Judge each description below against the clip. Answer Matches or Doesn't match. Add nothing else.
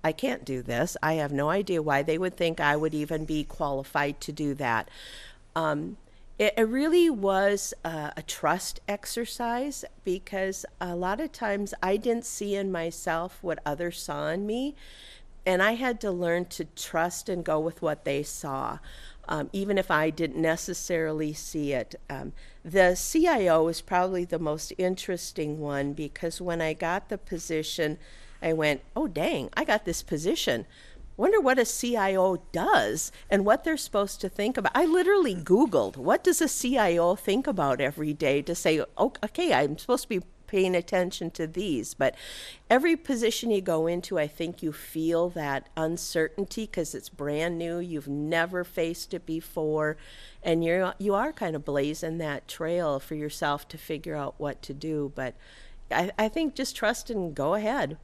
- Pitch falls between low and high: Matches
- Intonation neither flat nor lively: Matches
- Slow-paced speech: Doesn't match